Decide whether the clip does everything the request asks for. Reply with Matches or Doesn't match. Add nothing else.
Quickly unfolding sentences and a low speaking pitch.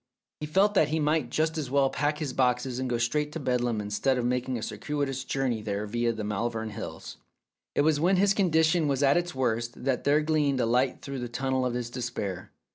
Matches